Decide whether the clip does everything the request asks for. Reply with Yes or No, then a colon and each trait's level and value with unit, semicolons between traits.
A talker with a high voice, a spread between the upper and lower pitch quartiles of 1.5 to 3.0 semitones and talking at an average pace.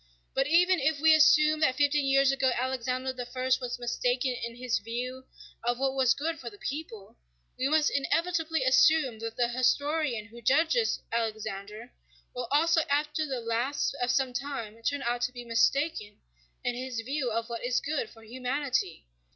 No: very high, 255 Hz; average, 3.5 semitones; average, 170 wpm